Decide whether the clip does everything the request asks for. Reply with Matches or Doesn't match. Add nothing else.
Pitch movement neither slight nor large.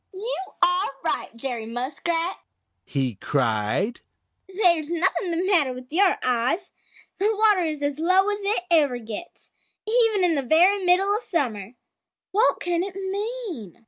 Doesn't match